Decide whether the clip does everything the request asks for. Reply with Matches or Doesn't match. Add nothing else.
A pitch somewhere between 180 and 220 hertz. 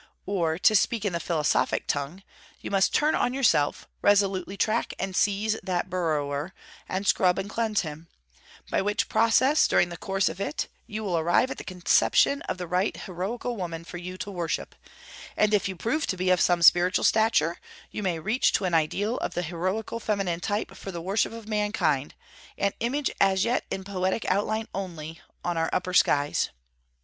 Matches